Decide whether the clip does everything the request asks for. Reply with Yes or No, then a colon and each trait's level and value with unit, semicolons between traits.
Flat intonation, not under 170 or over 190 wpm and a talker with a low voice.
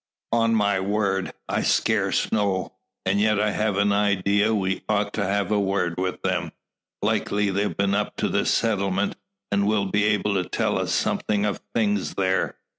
Yes: narrow, 1.4 semitones; average, 180 wpm; low, 100 Hz